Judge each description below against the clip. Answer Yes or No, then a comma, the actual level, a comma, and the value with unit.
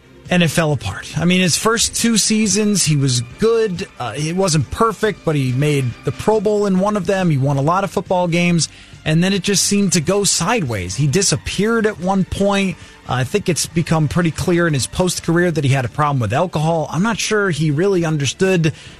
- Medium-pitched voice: Yes, medium, 175 Hz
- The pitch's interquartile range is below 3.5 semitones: No, average, 5.0 semitones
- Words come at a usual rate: No, fast, 225 wpm